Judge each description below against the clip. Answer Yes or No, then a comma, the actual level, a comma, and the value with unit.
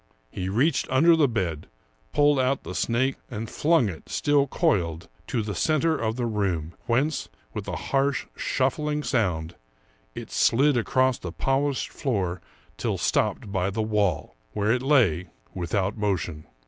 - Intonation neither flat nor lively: No, wide, 6.5 semitones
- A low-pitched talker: Yes, low, 115 Hz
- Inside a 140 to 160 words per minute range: Yes, average, 155 wpm